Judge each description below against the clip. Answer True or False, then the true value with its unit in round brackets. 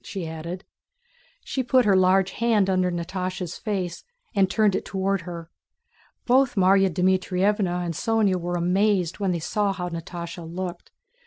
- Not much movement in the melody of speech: True (2.2 semitones)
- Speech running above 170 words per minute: False (150 wpm)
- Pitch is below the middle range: False (185 Hz)